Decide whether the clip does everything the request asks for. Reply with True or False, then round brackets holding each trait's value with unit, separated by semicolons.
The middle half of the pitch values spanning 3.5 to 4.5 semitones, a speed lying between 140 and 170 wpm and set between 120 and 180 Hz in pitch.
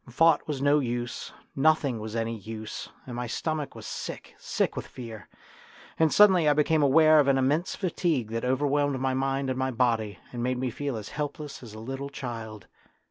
False (3.8 semitones; 190 wpm; 135 Hz)